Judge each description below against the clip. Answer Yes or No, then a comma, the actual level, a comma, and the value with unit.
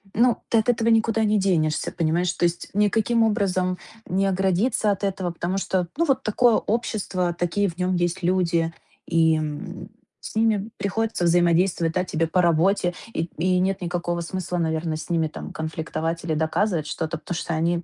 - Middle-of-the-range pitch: Yes, medium, 180 Hz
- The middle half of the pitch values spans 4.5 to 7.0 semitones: No, average, 3.3 semitones